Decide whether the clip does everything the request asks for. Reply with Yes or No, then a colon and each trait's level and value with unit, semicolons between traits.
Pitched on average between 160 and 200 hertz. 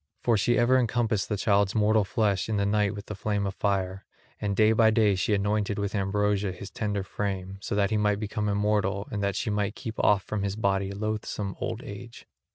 No: low, 105 Hz